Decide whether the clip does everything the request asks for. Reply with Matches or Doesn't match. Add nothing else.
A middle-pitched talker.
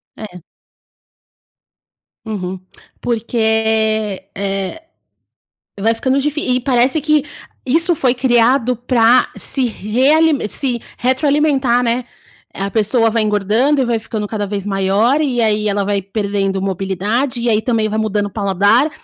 Doesn't match